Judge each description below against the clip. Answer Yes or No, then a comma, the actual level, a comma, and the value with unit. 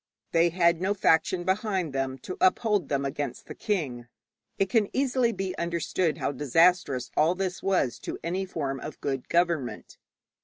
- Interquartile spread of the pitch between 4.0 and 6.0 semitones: Yes, average, 5.0 semitones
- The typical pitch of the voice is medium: Yes, medium, 170 Hz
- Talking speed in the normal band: Yes, average, 160 wpm